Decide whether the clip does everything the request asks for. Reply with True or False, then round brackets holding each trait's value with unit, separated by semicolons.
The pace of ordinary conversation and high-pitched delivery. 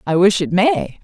False (235 wpm; 195 Hz)